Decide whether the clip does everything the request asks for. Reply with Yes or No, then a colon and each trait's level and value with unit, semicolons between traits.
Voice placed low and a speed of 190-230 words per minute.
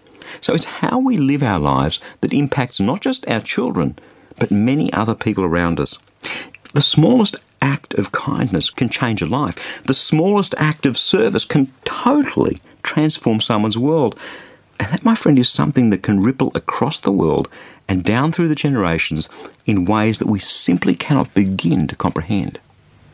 No: low, 130 Hz; average, 165 wpm